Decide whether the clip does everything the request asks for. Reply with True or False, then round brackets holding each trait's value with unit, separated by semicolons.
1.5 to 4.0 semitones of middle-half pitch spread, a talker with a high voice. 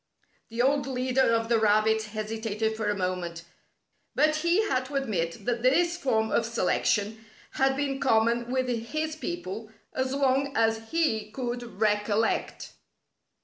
True (3.7 semitones; 230 Hz)